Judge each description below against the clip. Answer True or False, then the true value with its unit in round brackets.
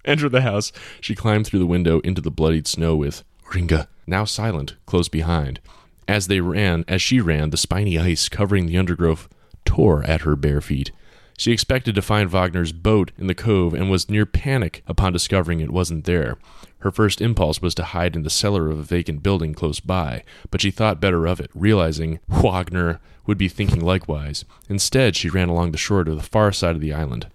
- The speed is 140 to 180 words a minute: False (205 wpm)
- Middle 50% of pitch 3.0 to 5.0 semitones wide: True (3.7 semitones)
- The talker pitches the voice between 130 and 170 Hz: False (90 Hz)